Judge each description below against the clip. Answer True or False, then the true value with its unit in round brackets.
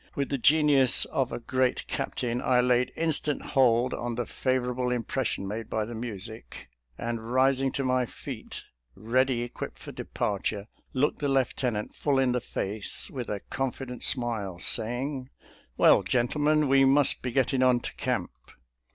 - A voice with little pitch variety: True (2.3 semitones)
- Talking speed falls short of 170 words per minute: True (160 wpm)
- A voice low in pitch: True (125 Hz)